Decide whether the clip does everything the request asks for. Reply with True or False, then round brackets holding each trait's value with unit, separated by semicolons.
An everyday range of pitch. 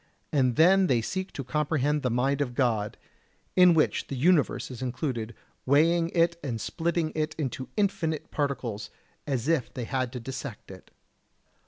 True (4.7 semitones)